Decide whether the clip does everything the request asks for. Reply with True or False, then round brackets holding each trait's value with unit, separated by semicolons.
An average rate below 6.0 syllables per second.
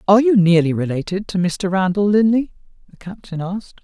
True (5.7 syllables/s)